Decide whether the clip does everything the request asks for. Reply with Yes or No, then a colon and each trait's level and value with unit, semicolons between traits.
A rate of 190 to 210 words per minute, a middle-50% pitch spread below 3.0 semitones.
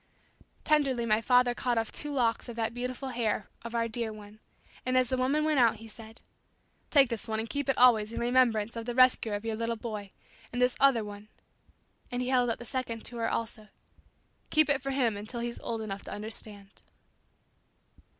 Yes: fast, 205 wpm; narrow, 2.5 semitones